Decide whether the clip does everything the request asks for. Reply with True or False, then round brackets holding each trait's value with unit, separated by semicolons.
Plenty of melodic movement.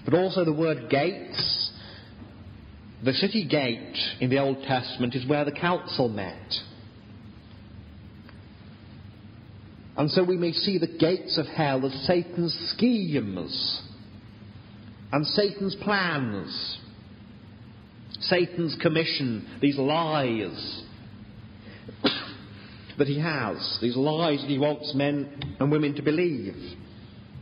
True (6.3 semitones)